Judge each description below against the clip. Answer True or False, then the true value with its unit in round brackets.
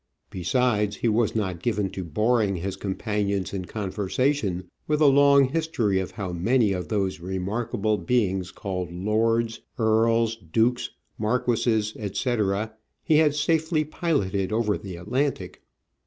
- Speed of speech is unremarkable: False (130 wpm)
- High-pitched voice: False (110 Hz)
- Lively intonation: False (4.1 semitones)